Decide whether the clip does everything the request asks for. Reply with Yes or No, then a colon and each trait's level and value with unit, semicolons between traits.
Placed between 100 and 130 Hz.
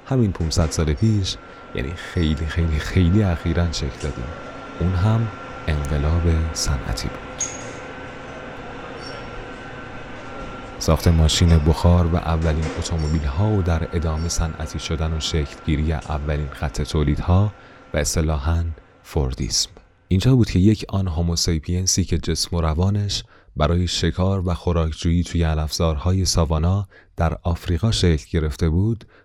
No: very low, 85 Hz